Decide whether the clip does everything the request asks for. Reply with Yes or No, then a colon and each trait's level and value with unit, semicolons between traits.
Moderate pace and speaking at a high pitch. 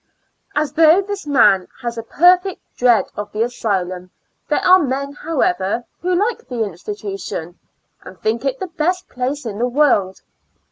Yes: average, 155 wpm; very high, 250 Hz